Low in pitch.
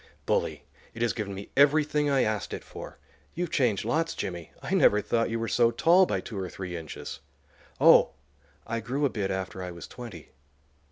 Yes: low, 115 Hz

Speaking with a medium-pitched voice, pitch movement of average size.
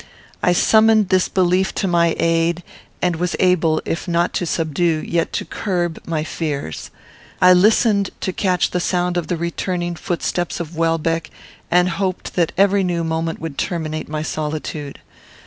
No: medium, 175 Hz; narrow, 1.9 semitones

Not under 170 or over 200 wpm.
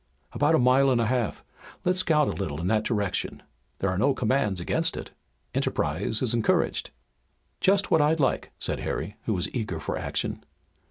Yes: average, 180 wpm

